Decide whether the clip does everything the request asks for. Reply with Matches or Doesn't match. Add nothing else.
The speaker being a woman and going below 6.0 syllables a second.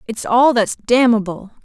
Matches